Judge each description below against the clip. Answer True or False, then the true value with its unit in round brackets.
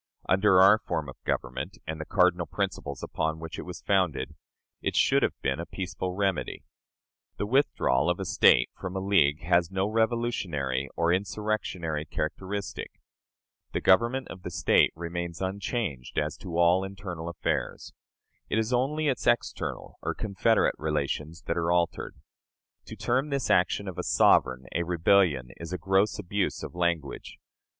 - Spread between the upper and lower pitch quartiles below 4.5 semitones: True (3.8 semitones)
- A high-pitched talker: False (90 Hz)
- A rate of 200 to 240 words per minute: False (160 wpm)